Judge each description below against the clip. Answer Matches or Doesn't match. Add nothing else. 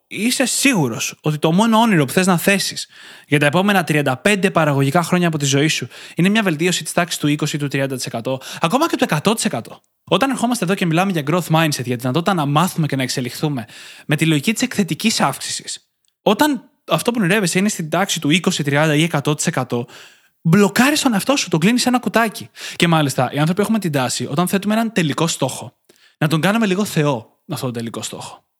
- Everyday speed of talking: Doesn't match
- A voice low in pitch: Doesn't match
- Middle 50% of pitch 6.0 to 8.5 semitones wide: Doesn't match